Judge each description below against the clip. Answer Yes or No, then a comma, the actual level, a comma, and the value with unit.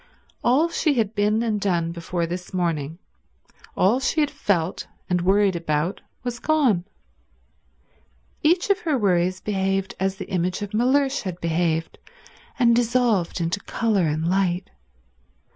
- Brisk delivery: No, average, 140 wpm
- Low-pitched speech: No, high, 195 Hz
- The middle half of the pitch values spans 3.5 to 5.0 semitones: No, wide, 5.4 semitones